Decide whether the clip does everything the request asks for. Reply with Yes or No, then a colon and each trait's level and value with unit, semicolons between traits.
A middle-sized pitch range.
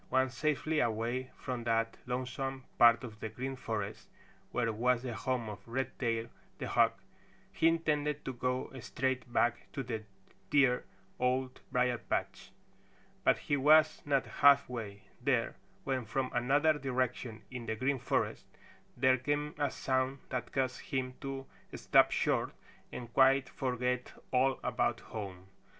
No: narrow, 2.2 semitones